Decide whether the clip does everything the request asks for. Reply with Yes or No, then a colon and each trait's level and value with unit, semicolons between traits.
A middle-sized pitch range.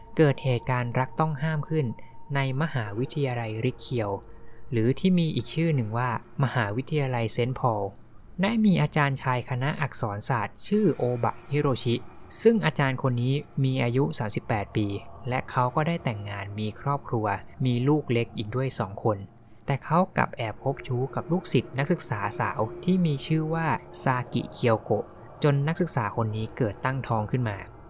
Yes: average, 4.1 semitones